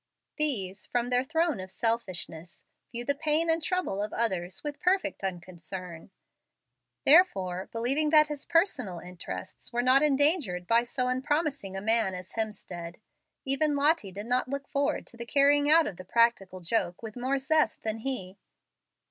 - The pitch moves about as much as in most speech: No, wide, 7.4 semitones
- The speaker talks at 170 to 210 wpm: No, average, 160 wpm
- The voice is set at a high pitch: Yes, high, 240 Hz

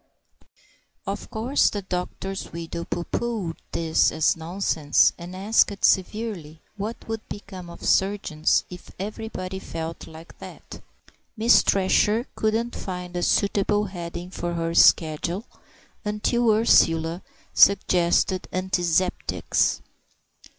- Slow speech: Yes, slow, 110 wpm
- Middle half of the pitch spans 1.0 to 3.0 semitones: No, average, 3.6 semitones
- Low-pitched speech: No, medium, 185 Hz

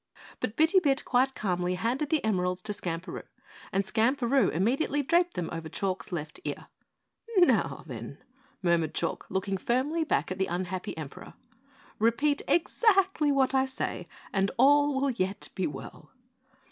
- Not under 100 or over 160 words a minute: Yes, average, 145 wpm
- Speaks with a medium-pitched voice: No, high, 230 Hz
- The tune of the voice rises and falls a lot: Yes, wide, 7.6 semitones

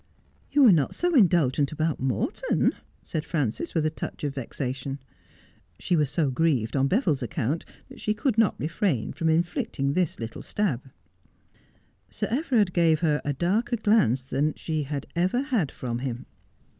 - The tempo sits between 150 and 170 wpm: Yes, average, 165 wpm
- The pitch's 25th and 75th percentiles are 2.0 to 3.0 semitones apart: No, wide, 5.5 semitones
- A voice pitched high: No, medium, 155 Hz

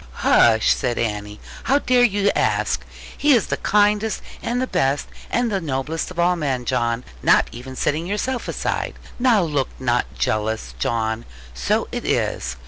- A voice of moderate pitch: Yes, medium, 145 Hz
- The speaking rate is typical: Yes, average, 160 wpm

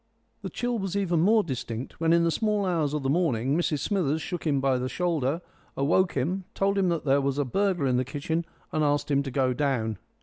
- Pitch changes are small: No, average, 4.8 semitones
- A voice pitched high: No, medium, 155 Hz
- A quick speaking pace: Yes, fast, 230 wpm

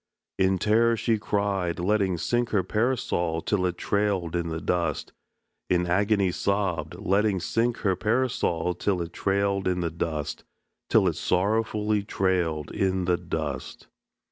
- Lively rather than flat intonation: No, average, 3.1 semitones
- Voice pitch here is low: Yes, very low, 95 Hz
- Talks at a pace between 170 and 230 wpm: No, average, 140 wpm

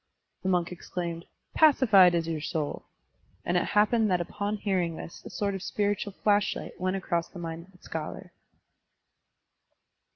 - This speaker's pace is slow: No, average, 155 wpm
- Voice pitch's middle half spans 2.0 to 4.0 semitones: Yes, average, 3.3 semitones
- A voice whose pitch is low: No, medium, 185 Hz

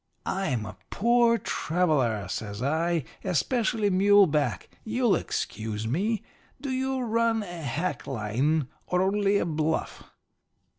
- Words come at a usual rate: No, slow, 120 wpm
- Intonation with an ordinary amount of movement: No, wide, 7.6 semitones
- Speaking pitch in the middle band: Yes, medium, 180 Hz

